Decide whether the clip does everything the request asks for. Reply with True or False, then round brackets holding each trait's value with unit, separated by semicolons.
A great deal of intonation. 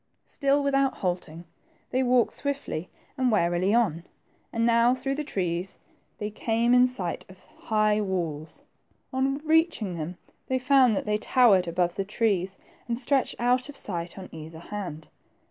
True (6.1 semitones)